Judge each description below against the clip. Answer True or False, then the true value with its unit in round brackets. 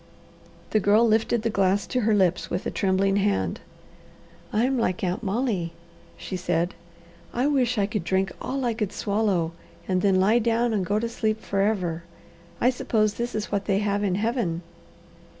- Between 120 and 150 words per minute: False (175 wpm)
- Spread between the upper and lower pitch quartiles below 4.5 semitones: True (3.3 semitones)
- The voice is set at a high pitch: True (205 Hz)